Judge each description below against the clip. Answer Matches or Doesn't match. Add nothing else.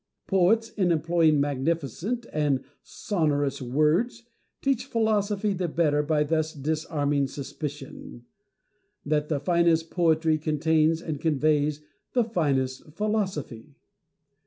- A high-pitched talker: Doesn't match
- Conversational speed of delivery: Doesn't match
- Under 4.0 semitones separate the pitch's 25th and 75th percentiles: Matches